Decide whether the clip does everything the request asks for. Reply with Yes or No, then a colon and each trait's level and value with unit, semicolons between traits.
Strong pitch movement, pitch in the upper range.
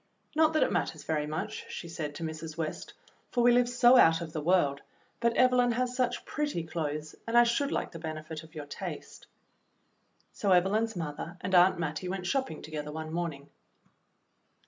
No: wide, 7.3 semitones; medium, 170 Hz